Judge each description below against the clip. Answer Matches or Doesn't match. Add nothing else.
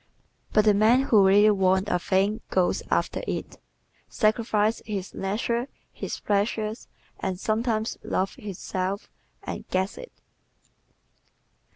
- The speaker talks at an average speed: Doesn't match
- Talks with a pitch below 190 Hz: Doesn't match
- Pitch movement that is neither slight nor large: Doesn't match